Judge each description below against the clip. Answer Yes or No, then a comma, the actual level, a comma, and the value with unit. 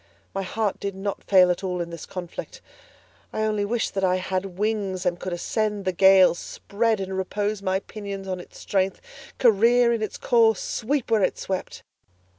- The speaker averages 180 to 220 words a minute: Yes, average, 185 wpm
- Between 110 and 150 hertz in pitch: No, high, 195 Hz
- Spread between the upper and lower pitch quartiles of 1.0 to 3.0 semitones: Yes, narrow, 2.6 semitones